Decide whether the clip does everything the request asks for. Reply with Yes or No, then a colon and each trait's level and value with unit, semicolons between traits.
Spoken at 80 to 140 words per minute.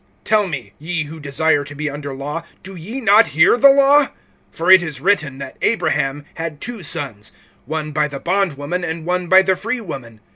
No: average, 190 wpm